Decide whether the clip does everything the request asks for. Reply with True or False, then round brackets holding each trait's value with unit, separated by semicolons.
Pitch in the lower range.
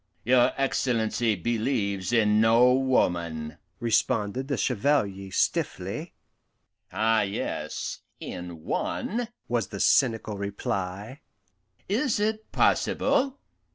True (115 Hz)